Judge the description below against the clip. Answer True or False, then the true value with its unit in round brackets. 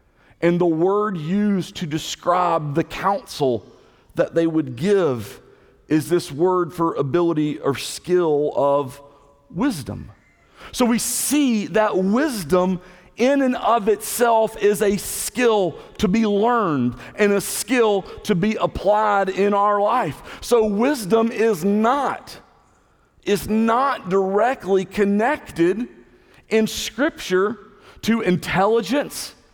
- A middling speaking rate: False (115 wpm)